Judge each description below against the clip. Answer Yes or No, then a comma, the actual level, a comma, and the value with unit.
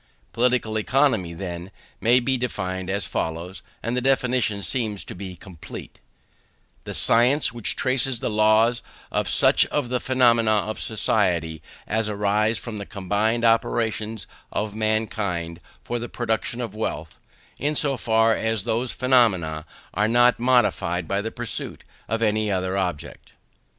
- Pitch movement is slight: No, average, 3.5 semitones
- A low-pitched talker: Yes, low, 110 Hz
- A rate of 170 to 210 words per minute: No, average, 145 wpm